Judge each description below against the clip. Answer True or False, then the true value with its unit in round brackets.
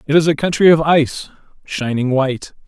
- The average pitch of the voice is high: False (145 Hz)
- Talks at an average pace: True (180 wpm)